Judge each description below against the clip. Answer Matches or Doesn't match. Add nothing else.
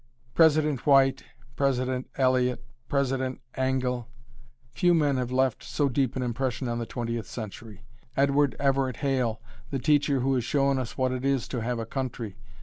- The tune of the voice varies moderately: Doesn't match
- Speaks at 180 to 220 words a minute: Doesn't match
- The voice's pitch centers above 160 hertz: Doesn't match